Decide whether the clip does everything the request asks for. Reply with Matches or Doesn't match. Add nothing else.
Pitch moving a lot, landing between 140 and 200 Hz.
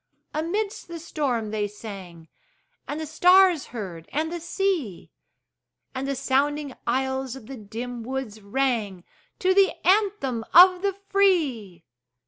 Doesn't match